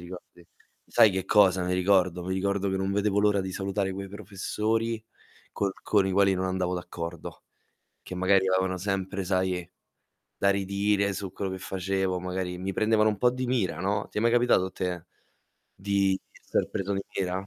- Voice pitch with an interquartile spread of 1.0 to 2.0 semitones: Yes, narrow, 1.4 semitones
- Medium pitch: No, very low, 95 Hz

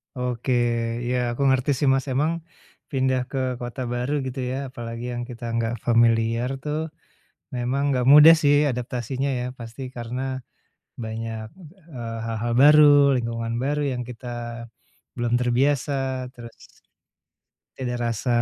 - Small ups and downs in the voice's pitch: Yes, narrow, 2.3 semitones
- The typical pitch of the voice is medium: No, low, 125 Hz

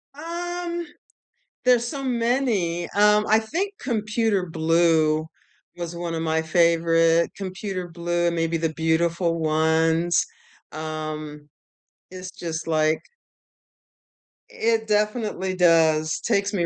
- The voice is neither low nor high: Yes, medium, 170 Hz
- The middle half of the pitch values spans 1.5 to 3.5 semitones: No, average, 4.7 semitones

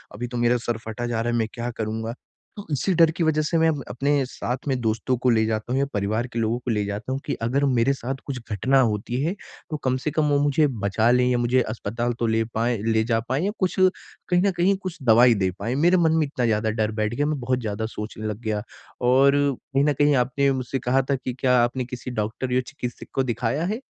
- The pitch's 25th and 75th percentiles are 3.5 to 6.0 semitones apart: Yes, average, 3.8 semitones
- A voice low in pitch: Yes, low, 125 Hz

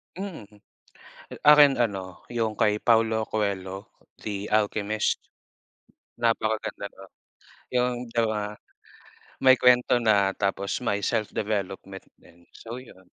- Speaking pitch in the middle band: No, low, 110 Hz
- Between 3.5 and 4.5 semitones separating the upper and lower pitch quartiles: No, average, 2.9 semitones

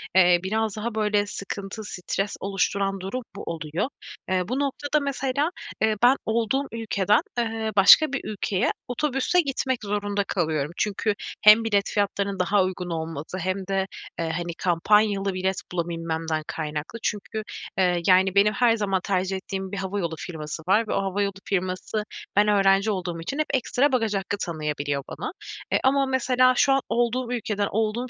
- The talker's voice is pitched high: Yes, high, 200 Hz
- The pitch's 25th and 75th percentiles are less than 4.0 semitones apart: Yes, average, 3.5 semitones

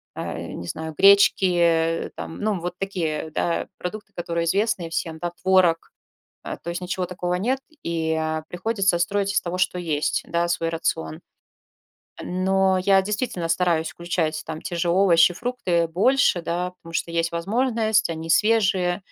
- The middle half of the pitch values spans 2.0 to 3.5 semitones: Yes, average, 2.7 semitones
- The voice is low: No, medium, 175 Hz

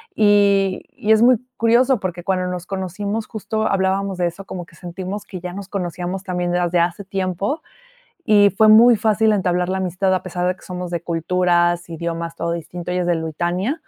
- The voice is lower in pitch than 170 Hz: No, medium, 185 Hz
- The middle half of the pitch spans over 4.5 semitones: No, narrow, 2.5 semitones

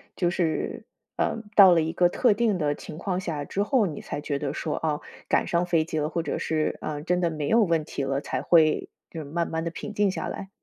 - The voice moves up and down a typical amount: Yes, average, 3.1 semitones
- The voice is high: No, medium, 165 Hz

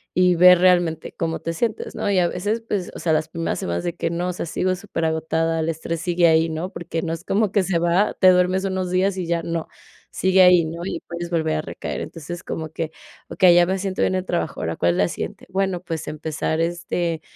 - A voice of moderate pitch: Yes, medium, 170 Hz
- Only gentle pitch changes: Yes, narrow, 2.1 semitones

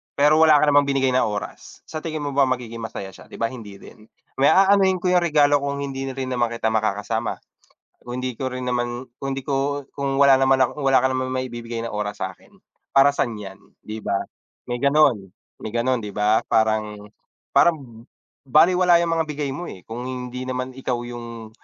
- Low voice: Yes, low, 130 Hz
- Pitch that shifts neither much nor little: Yes, average, 3.5 semitones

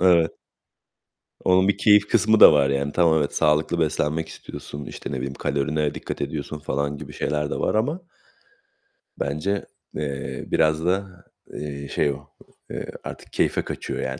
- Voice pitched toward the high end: No, very low, 75 Hz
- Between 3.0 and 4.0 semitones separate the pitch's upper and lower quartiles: Yes, average, 3.7 semitones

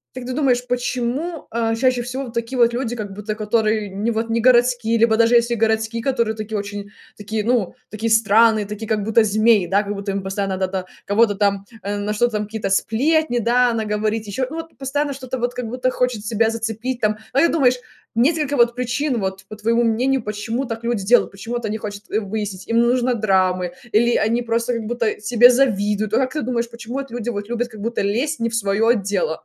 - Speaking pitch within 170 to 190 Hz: No, high, 230 Hz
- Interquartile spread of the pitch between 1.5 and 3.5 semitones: Yes, narrow, 2.6 semitones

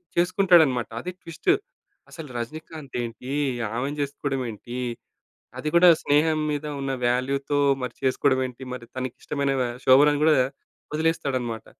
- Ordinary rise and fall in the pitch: Yes, average, 3.5 semitones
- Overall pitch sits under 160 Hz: Yes, medium, 140 Hz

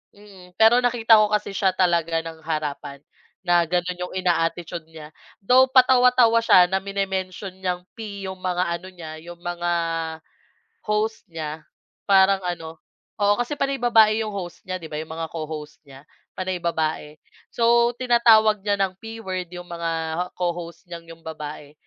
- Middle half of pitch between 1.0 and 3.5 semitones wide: No, average, 4.3 semitones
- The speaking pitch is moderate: Yes, medium, 180 Hz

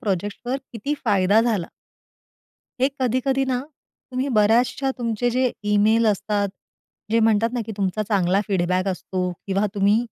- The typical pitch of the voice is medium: No, high, 215 Hz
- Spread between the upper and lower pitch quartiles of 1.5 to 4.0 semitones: Yes, average, 3.6 semitones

